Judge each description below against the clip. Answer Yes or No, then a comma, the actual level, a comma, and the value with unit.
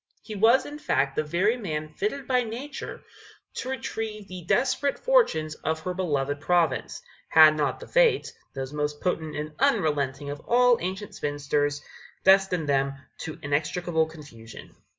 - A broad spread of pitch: Yes, wide, 6.8 semitones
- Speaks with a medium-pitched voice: Yes, medium, 160 Hz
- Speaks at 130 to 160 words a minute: Yes, average, 150 wpm